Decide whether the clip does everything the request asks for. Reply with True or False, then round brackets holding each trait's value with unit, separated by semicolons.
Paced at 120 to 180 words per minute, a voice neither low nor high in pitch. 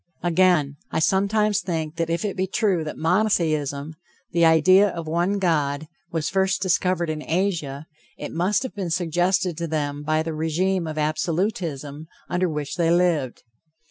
True (160 wpm; 170 Hz)